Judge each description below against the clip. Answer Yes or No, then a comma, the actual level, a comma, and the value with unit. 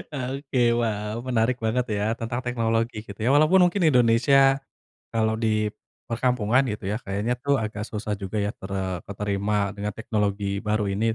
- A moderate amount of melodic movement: Yes, average, 3.0 semitones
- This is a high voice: No, low, 110 Hz